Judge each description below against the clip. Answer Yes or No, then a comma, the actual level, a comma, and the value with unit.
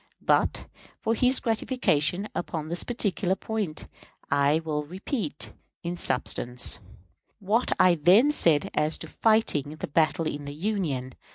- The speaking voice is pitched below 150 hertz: No, medium, 170 Hz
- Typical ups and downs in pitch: No, wide, 6.4 semitones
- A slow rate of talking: Yes, slow, 130 wpm